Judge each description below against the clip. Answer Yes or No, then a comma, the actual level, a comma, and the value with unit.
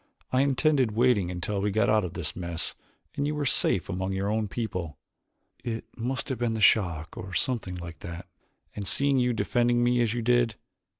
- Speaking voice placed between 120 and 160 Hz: No, low, 110 Hz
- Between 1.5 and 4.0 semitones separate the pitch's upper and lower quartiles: No, average, 4.7 semitones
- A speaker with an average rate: Yes, average, 195 wpm